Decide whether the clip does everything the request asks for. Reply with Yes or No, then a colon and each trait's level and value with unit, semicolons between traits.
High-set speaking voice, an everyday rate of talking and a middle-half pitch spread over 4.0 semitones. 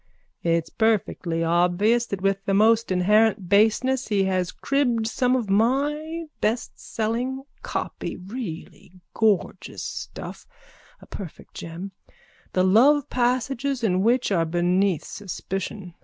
No: high, 210 Hz; slow, 115 wpm; average, 4.9 semitones